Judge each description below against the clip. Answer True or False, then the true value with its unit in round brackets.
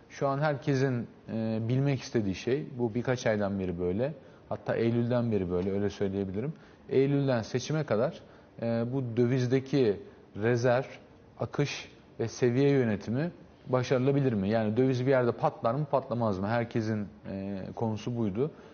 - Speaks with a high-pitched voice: False (120 Hz)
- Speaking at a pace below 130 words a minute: False (140 wpm)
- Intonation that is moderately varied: True (3.5 semitones)